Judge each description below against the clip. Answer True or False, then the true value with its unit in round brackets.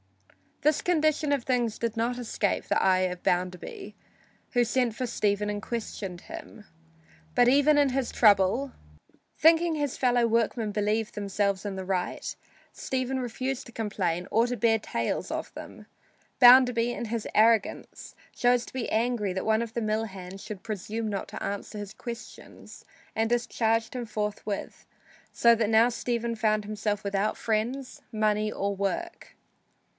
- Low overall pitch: False (225 Hz)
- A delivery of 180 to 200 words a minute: False (155 wpm)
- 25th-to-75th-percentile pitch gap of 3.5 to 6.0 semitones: False (2.9 semitones)